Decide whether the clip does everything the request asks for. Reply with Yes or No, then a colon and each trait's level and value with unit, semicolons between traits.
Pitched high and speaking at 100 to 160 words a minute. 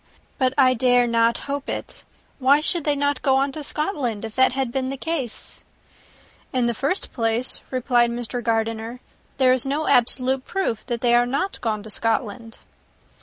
No: very high, 255 Hz; average, 175 wpm